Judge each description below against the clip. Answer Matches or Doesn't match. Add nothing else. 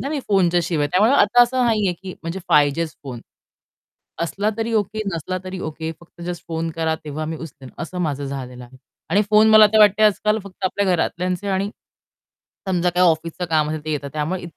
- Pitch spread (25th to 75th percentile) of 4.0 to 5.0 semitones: Matches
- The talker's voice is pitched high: Doesn't match